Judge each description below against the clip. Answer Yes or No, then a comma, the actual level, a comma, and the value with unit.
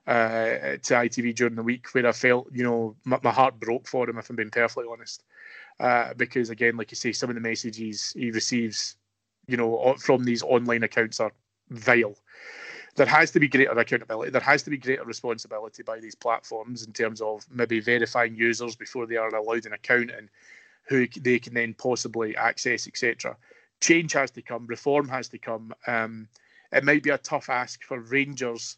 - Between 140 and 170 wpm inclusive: No, average, 195 wpm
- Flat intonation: Yes, narrow, 1.7 semitones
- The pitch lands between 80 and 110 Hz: No, low, 120 Hz